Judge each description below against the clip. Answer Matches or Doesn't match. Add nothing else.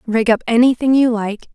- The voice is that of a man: Doesn't match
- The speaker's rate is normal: Matches